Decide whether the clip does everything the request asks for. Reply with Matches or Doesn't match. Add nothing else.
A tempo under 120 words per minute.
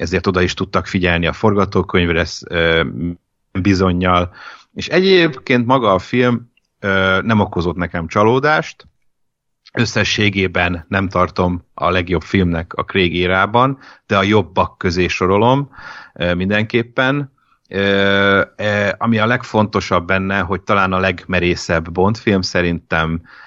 Matches